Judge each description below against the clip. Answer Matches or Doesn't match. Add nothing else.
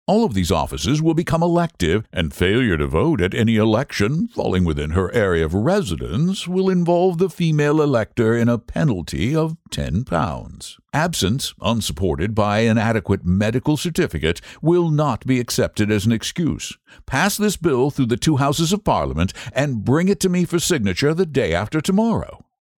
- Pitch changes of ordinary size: Doesn't match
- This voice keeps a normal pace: Matches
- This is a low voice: Matches